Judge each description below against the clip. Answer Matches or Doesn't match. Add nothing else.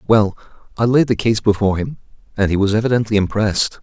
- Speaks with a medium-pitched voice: Doesn't match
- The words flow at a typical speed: Matches